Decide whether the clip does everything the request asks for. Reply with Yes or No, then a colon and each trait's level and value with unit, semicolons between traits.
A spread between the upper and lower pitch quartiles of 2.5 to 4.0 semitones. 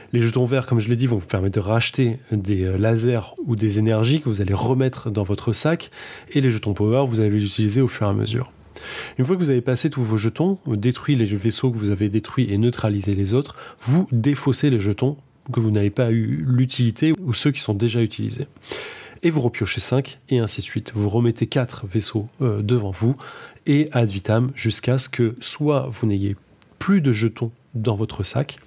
Yes: average, 3.3 semitones